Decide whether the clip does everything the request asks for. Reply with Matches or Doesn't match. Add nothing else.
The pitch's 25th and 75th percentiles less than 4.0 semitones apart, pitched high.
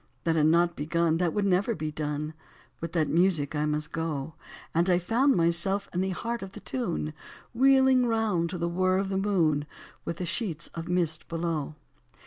Doesn't match